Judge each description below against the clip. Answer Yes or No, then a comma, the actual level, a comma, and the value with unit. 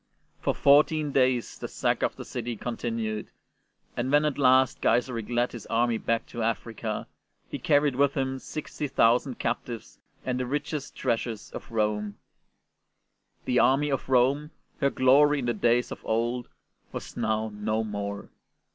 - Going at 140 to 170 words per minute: Yes, average, 155 wpm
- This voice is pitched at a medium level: No, low, 120 Hz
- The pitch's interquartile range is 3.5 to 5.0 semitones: No, average, 3.0 semitones